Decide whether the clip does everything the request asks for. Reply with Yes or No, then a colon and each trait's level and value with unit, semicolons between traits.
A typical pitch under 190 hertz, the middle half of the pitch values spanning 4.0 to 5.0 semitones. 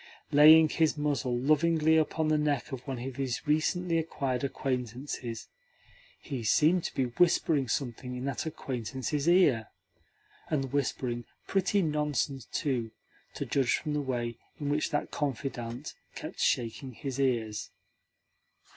No: medium, 140 Hz; average, 3.5 semitones